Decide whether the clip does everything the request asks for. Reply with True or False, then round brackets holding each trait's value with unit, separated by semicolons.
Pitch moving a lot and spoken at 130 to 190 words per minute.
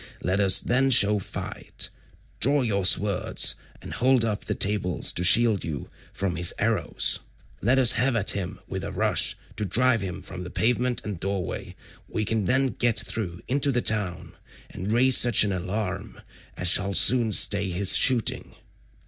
False (4.3 semitones; 170 wpm)